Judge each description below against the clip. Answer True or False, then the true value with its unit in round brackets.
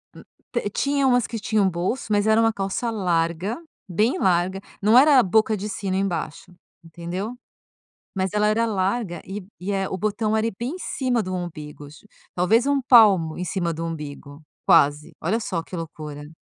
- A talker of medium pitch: False (195 Hz)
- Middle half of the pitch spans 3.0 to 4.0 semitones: False (4.6 semitones)